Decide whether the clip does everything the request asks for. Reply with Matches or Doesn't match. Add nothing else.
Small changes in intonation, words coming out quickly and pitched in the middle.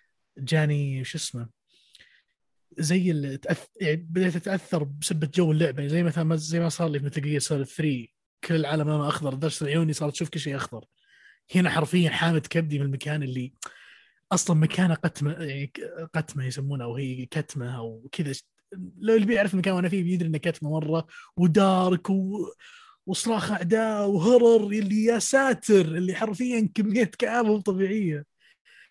Doesn't match